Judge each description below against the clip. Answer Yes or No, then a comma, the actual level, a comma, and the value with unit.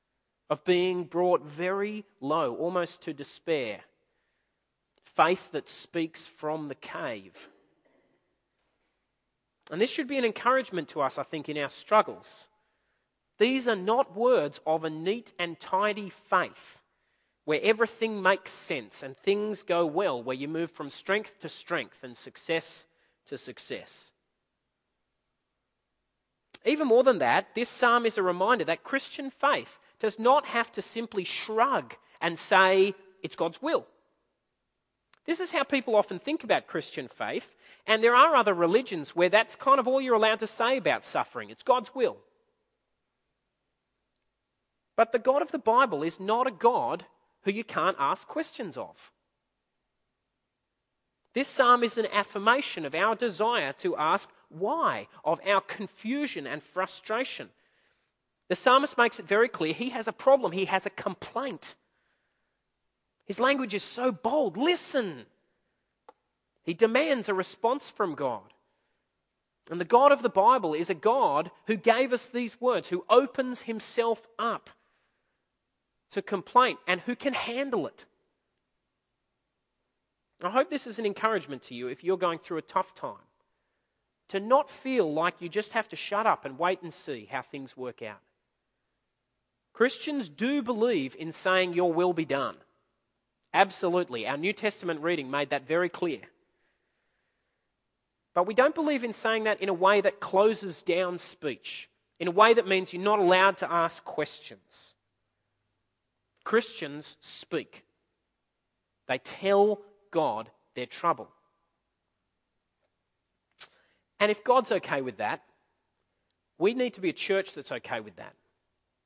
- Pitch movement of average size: No, wide, 6.1 semitones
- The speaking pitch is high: Yes, high, 200 Hz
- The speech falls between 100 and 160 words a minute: Yes, average, 145 wpm